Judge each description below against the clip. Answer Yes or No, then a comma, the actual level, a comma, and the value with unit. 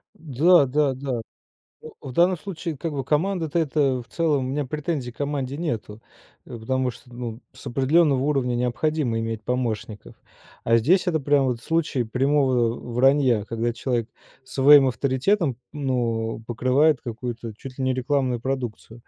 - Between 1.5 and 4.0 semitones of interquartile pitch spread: Yes, average, 3.6 semitones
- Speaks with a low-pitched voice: Yes, low, 130 Hz